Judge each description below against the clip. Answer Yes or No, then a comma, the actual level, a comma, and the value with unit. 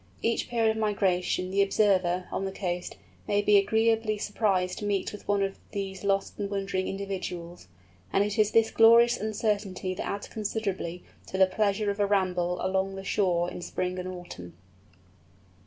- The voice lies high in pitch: Yes, high, 195 Hz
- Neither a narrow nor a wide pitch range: No, narrow, 2.2 semitones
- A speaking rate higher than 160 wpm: Yes, average, 170 wpm